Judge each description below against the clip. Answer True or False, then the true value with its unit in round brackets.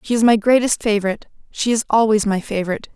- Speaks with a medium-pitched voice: False (215 Hz)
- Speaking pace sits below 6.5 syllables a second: False (7.0 syllables/s)